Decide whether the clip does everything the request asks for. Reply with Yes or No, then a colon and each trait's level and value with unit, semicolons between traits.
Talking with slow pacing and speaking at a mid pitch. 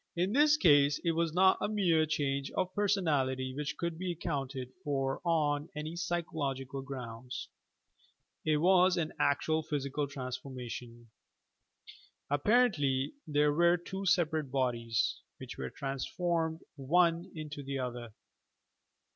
Yes: slow, 125 wpm; medium, 150 Hz